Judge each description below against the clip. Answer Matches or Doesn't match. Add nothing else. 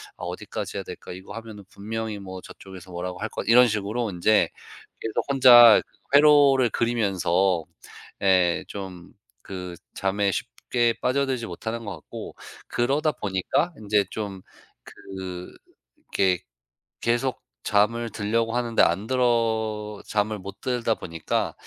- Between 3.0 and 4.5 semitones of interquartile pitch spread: Matches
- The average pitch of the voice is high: Doesn't match